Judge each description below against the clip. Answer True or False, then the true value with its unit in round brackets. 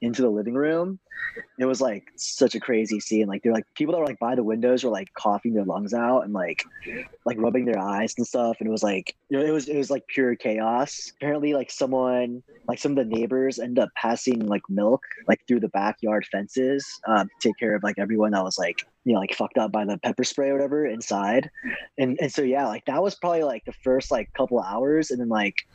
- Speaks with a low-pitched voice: True (120 Hz)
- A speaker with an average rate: False (245 wpm)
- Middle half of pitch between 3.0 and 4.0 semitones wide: True (3.6 semitones)